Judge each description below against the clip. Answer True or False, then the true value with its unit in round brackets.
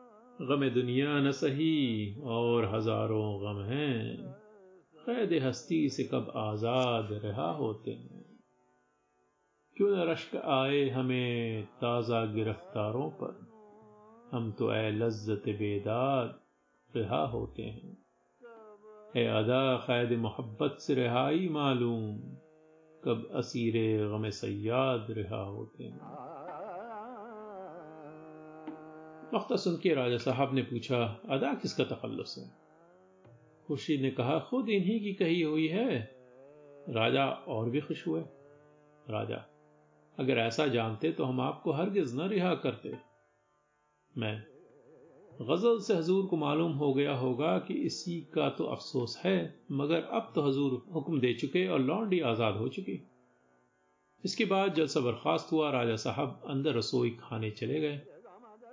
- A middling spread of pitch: False (5.8 semitones)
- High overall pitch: False (135 Hz)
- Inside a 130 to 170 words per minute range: False (120 wpm)